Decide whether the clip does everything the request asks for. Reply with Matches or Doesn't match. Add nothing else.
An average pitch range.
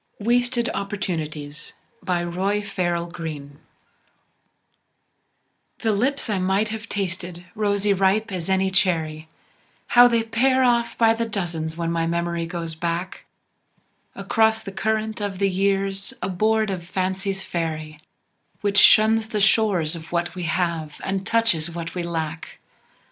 Matches